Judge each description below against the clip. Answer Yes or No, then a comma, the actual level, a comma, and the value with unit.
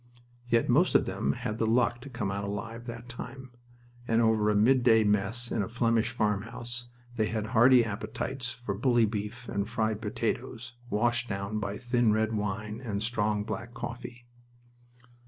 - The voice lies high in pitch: No, low, 115 Hz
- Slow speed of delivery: No, average, 165 wpm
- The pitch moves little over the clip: Yes, narrow, 2.3 semitones